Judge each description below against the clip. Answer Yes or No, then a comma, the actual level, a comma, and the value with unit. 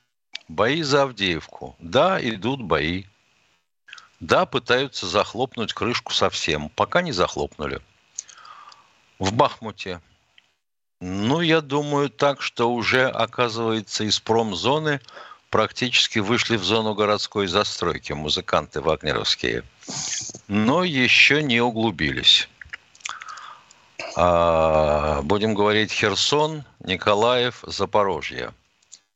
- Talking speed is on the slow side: Yes, slow, 90 wpm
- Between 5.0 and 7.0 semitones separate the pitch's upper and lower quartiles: Yes, wide, 5.6 semitones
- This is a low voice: Yes, low, 110 Hz